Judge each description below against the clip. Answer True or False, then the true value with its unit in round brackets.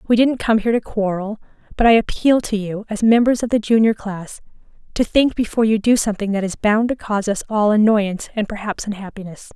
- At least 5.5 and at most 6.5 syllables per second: True (6.0 syllables/s)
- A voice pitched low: False (215 Hz)